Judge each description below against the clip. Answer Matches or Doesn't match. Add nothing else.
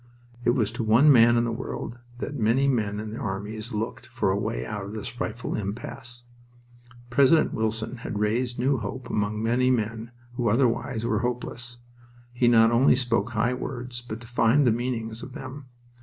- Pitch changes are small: Matches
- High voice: Doesn't match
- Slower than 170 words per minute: Doesn't match